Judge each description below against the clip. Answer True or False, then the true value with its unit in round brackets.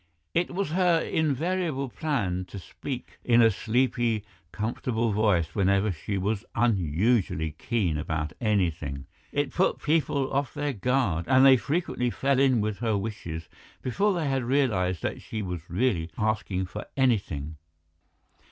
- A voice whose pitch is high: False (110 Hz)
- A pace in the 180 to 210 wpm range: False (145 wpm)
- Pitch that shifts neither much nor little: False (6.5 semitones)